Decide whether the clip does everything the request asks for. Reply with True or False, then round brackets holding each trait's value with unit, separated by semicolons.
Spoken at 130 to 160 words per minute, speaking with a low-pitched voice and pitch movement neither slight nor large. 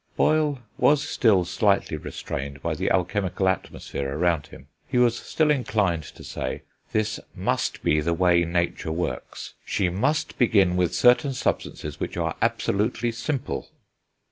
False (145 wpm; 100 Hz; 6.1 semitones)